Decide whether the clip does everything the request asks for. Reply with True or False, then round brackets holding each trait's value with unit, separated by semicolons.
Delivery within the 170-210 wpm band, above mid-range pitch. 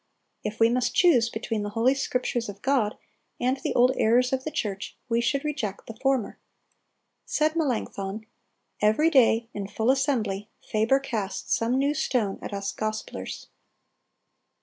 False (150 wpm; 235 Hz)